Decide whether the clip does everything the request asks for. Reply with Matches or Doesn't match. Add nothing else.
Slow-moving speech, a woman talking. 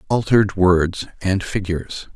Doesn't match